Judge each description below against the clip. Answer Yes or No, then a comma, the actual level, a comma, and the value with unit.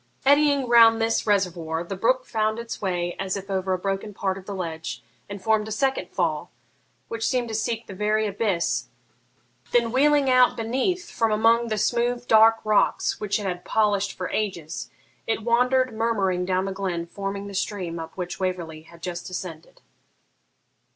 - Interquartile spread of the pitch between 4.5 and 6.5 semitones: No, average, 3.8 semitones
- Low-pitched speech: No, high, 205 Hz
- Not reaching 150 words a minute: No, average, 175 wpm